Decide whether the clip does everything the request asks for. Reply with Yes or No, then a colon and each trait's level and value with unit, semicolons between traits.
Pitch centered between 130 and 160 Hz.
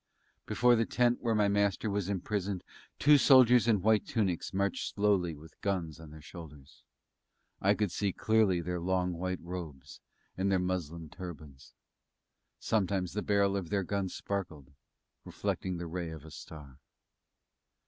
No: very low, 95 Hz